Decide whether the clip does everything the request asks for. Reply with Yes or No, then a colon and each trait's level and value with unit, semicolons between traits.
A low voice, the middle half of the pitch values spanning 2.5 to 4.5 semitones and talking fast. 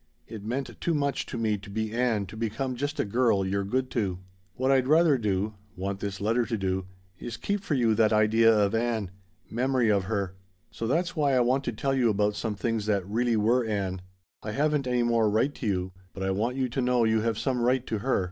Yes: low, 115 Hz; average, 3.6 semitones; fast, 235 wpm